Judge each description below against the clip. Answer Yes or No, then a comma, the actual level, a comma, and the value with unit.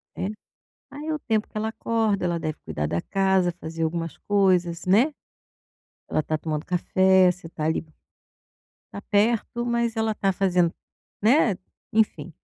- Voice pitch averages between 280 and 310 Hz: No, high, 190 Hz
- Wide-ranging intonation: No, average, 4.7 semitones